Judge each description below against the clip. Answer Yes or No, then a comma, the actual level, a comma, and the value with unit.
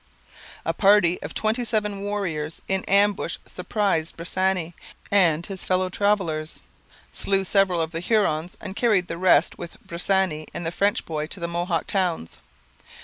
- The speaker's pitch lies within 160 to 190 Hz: Yes, medium, 185 Hz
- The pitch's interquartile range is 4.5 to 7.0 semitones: No, average, 3.1 semitones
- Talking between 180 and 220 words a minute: No, average, 150 wpm